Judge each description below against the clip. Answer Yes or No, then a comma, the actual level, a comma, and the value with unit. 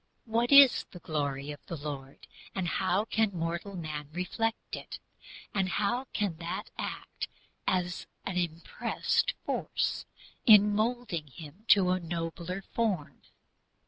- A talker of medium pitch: Yes, medium, 180 Hz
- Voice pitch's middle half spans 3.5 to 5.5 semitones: Yes, average, 4.3 semitones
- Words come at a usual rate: No, slow, 130 wpm